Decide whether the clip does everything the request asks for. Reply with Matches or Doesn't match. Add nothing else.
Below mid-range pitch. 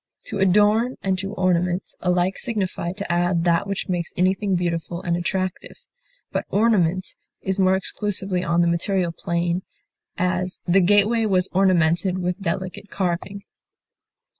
Doesn't match